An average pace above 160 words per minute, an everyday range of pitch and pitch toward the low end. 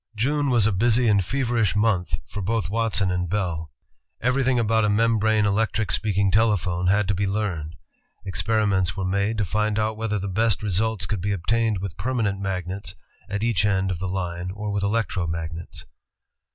Yes: average, 180 wpm; average, 3.0 semitones; low, 105 Hz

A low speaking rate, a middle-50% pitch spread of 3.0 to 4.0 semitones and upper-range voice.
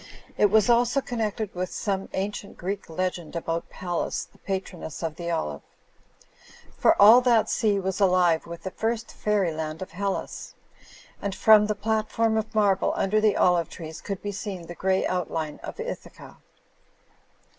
No: average, 155 wpm; average, 3.6 semitones; high, 195 Hz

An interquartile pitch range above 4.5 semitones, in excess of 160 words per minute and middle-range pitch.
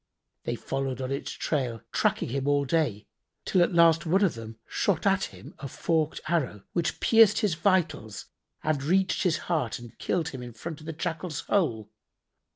Yes: average, 5.2 semitones; average, 180 wpm; medium, 155 Hz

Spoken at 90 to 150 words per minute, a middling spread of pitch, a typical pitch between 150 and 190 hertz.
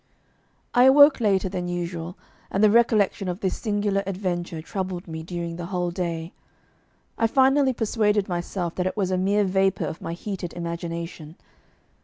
No: average, 160 wpm; average, 3.1 semitones; medium, 185 Hz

